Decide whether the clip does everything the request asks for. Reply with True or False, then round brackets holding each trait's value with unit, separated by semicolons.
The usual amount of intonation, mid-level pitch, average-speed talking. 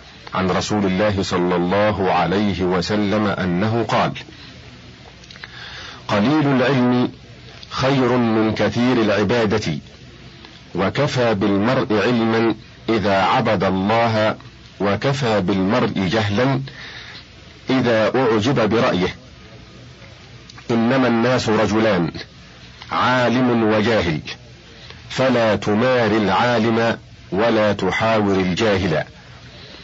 False (3.2 semitones; 110 Hz; 75 wpm)